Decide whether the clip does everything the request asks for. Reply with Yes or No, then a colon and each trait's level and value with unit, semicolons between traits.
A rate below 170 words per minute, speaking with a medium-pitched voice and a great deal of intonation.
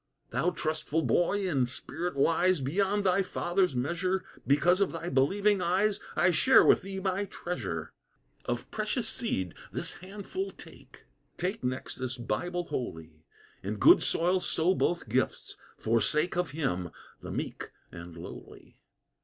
Yes: average, 145 wpm; medium, 175 Hz; wide, 6.3 semitones